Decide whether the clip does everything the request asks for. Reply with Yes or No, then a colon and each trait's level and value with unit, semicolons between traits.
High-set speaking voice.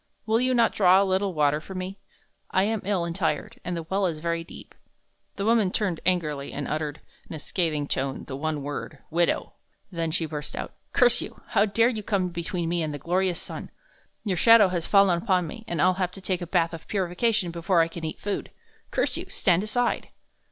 No: medium, 180 Hz